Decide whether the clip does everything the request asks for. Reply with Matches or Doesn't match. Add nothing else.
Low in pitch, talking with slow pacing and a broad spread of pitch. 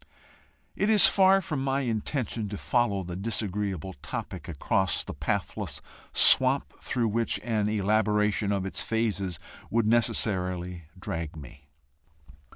Doesn't match